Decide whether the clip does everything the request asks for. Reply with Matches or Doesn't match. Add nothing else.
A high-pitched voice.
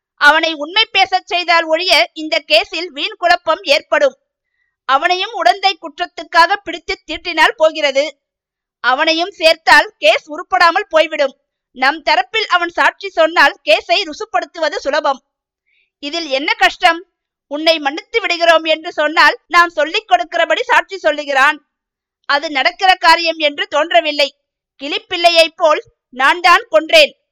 Matches